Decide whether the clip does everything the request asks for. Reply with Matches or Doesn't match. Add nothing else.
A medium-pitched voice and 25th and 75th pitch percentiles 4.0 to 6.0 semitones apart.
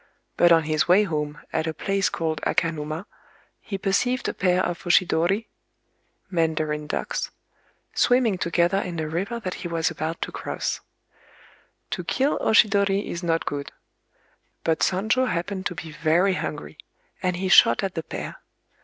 Doesn't match